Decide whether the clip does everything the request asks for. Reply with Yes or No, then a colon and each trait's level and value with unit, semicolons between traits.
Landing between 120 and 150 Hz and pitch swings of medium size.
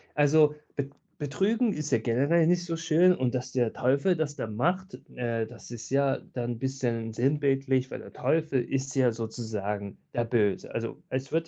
Yes: low, 135 Hz; average, 4.6 semitones